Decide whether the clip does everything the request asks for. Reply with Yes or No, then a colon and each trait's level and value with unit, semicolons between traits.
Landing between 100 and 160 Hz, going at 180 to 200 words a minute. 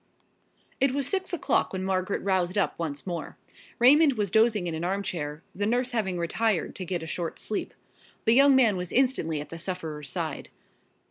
No: high, 190 Hz; average, 185 wpm